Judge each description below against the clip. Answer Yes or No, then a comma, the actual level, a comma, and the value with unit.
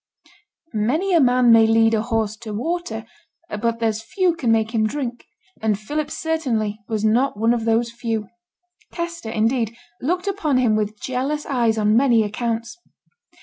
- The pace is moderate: Yes, average, 160 wpm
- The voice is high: Yes, high, 230 Hz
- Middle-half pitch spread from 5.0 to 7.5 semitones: No, average, 3.8 semitones